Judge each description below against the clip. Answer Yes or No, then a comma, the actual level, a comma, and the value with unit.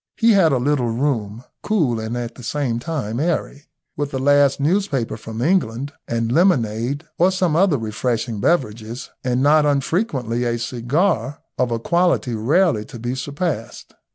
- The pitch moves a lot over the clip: No, average, 4.9 semitones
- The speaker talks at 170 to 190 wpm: No, average, 155 wpm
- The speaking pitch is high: No, low, 130 Hz